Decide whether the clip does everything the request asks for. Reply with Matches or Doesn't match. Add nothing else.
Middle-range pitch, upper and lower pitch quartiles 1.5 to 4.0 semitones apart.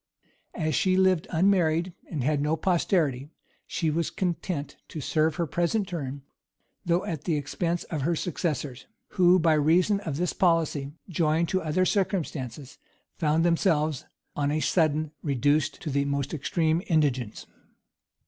Matches